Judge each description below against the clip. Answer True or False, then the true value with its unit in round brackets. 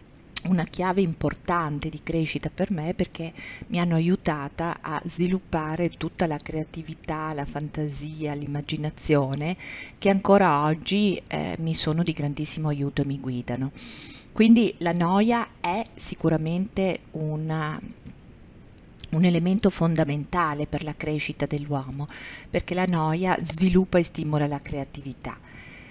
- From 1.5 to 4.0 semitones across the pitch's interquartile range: True (3.2 semitones)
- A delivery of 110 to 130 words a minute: True (120 wpm)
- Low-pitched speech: False (160 Hz)